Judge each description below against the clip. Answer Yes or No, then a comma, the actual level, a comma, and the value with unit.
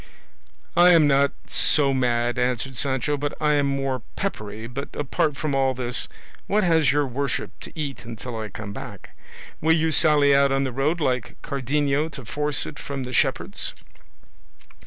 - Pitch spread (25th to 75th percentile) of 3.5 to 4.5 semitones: No, average, 2.8 semitones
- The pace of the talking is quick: No, average, 170 wpm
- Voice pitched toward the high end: No, medium, 140 Hz